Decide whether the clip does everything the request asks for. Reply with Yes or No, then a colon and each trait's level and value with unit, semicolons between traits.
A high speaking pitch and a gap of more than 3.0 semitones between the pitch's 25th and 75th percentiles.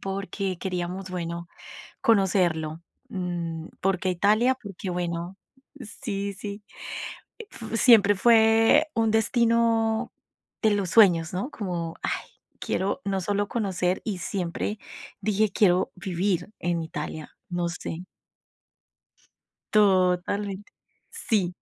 Yes: high, 195 Hz; average, 3.4 semitones